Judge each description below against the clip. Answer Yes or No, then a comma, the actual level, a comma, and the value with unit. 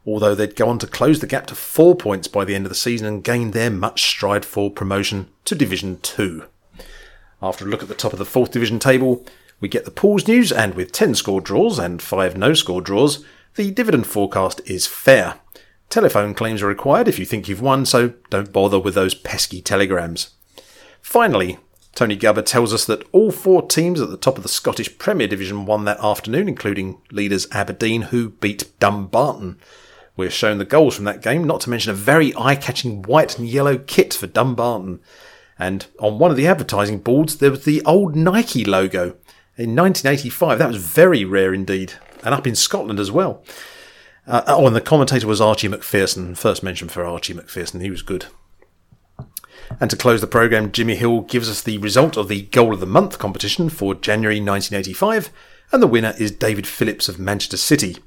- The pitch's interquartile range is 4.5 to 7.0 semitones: Yes, average, 5.2 semitones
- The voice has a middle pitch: No, low, 110 Hz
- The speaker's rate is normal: Yes, average, 195 wpm